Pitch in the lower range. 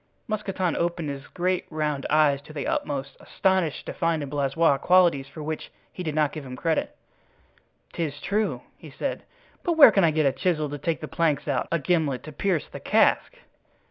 No: medium, 155 Hz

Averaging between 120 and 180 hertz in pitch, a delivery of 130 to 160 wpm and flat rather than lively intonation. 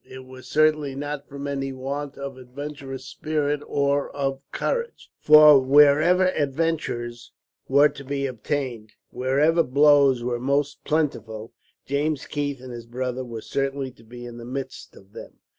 Yes: medium, 140 Hz; average, 150 wpm; narrow, 2.3 semitones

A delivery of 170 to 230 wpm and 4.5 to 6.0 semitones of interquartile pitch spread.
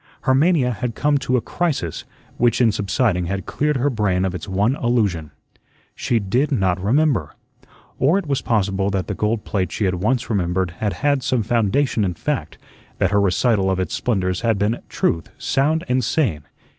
Yes: average, 185 wpm; average, 5.3 semitones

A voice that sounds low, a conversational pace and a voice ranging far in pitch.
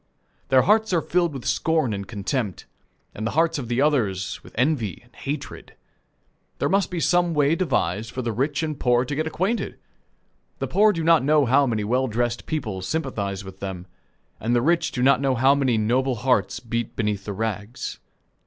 Yes: low, 130 Hz; average, 190 wpm; wide, 5.9 semitones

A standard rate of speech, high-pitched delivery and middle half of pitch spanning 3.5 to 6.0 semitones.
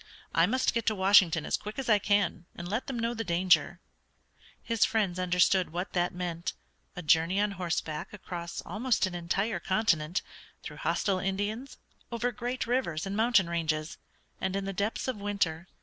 Yes: average, 175 wpm; high, 195 Hz; average, 4.0 semitones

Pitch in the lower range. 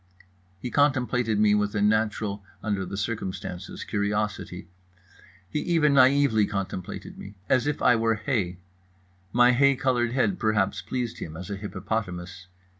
Yes: low, 110 Hz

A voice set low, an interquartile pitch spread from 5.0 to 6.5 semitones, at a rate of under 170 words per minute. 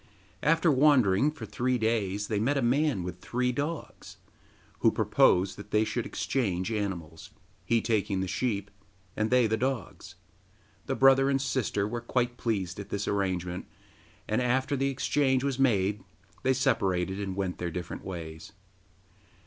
Yes: low, 110 Hz; average, 5.3 semitones; average, 155 wpm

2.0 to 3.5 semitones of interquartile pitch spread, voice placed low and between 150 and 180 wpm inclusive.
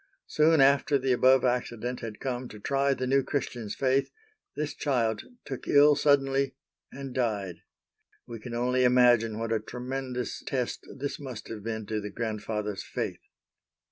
Yes: average, 3.2 semitones; low, 125 Hz; average, 155 wpm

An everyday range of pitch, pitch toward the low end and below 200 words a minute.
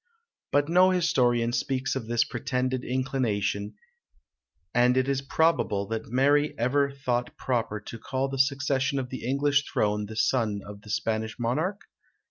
Yes: average, 3.3 semitones; low, 130 Hz; average, 155 wpm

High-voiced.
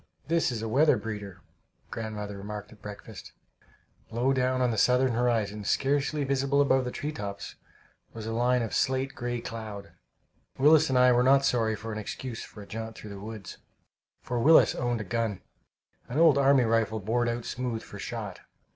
No: low, 120 Hz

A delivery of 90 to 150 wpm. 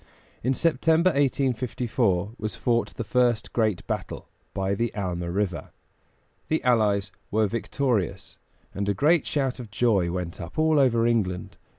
Yes: average, 145 wpm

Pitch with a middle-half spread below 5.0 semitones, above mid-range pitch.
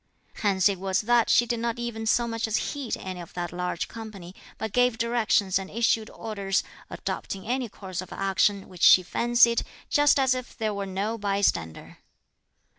Yes: average, 3.5 semitones; high, 215 Hz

